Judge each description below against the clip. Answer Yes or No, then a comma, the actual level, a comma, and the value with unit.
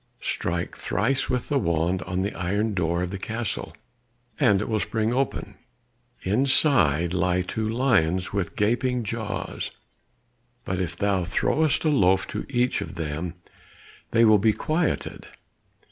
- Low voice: Yes, low, 100 Hz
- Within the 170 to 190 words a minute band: No, average, 145 wpm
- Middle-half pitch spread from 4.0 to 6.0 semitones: Yes, average, 4.9 semitones